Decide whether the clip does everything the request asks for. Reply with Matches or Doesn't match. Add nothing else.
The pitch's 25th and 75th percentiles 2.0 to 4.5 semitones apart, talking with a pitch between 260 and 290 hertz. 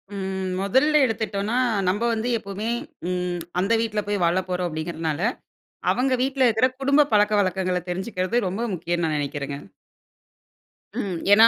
Doesn't match